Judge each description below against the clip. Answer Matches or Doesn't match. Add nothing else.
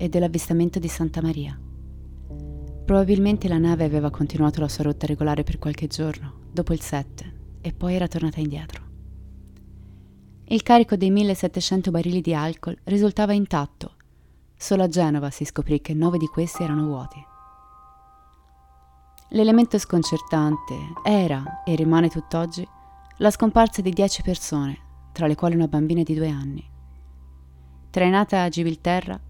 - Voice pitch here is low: Doesn't match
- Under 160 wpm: Matches